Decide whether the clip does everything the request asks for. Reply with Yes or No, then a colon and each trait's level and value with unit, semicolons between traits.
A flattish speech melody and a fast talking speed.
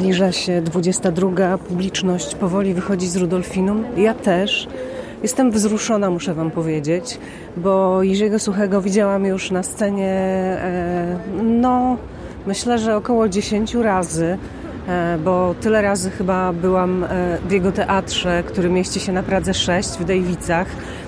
No: narrow, 2.1 semitones; average, 125 wpm